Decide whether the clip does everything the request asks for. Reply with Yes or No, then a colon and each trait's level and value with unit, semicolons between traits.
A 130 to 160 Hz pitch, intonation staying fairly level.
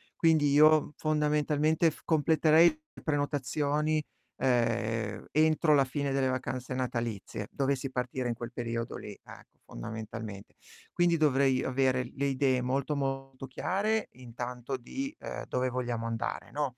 No: low, 135 Hz; average, 3.5 semitones